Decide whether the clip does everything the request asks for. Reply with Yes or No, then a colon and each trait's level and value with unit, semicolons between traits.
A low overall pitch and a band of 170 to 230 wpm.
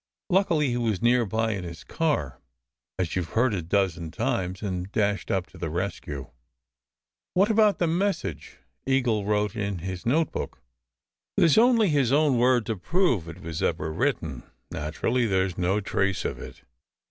Yes: low, 105 Hz; average, 175 wpm